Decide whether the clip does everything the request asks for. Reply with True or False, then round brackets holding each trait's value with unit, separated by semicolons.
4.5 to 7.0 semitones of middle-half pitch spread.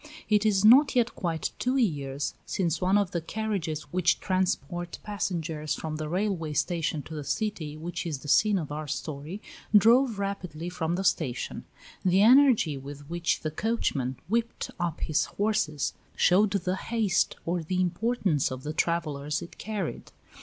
True (5.1 semitones)